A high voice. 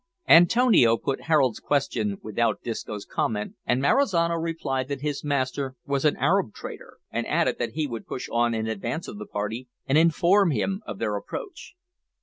No: low, 135 Hz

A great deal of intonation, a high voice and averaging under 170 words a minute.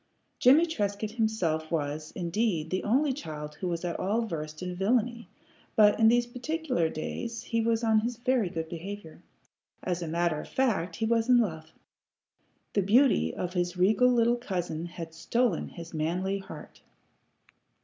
Yes: wide, 5.8 semitones; high, 195 Hz; average, 160 wpm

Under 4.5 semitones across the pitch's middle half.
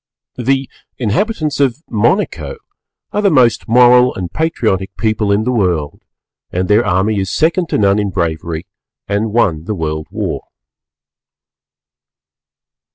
No: average, 5.3 semitones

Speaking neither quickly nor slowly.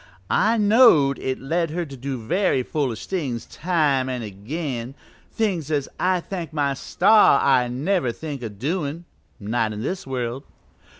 Yes: average, 155 wpm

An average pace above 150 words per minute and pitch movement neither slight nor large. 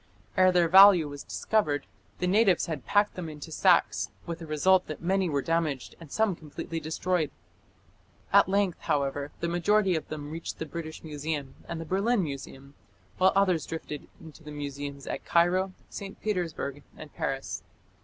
Yes: average, 165 wpm; average, 3.9 semitones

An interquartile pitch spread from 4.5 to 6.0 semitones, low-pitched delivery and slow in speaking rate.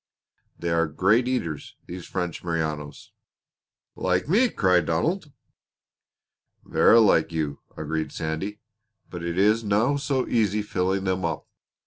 Yes: average, 4.8 semitones; very low, 90 Hz; slow, 125 wpm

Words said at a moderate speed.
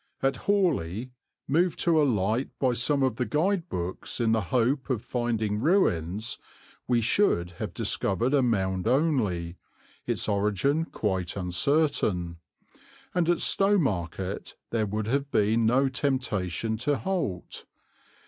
No: slow, 130 wpm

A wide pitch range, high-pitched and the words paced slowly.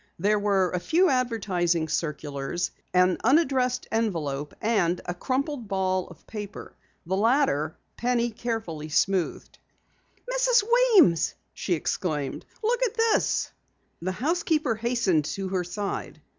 Yes: wide, 6.5 semitones; high, 205 Hz; slow, 120 wpm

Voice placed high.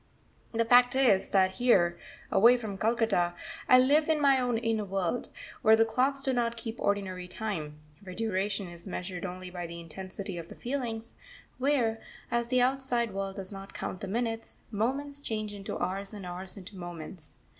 Yes: high, 215 Hz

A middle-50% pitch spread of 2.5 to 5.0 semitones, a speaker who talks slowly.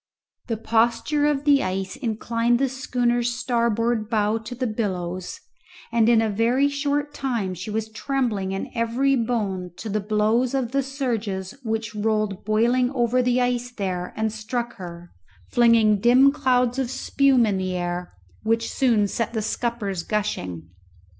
No: average, 3.0 semitones; average, 155 wpm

